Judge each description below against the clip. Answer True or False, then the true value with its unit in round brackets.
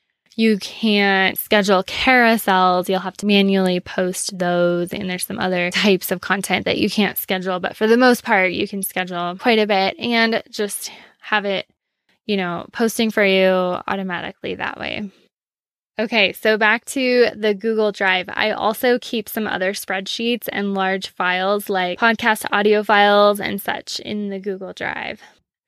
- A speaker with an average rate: True (165 wpm)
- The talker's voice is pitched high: True (200 Hz)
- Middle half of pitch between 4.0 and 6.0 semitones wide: False (2.6 semitones)